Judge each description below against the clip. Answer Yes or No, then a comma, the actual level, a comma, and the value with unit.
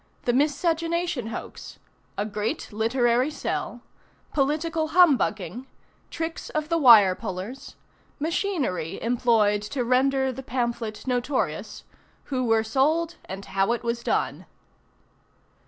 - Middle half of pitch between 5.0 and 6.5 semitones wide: Yes, average, 5.3 semitones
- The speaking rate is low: Yes, slow, 110 wpm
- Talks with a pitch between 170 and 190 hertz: No, very high, 250 Hz